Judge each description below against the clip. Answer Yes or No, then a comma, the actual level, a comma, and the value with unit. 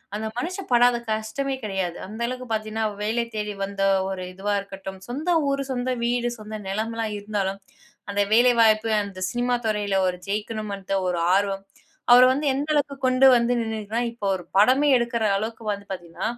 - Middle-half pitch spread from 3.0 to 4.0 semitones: Yes, average, 3.4 semitones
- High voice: Yes, high, 220 Hz